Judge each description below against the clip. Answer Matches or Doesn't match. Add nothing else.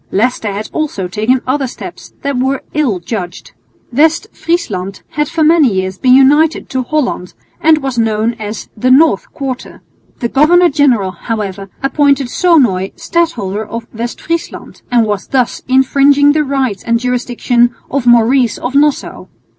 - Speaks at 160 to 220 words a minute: Doesn't match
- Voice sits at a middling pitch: Doesn't match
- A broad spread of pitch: Doesn't match